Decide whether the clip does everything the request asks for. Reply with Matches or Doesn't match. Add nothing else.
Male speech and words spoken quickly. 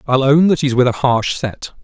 Matches